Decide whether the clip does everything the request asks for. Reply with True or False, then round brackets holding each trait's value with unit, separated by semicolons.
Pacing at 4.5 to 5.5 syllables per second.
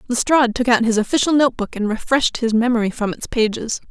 False (6.6 syllables/s)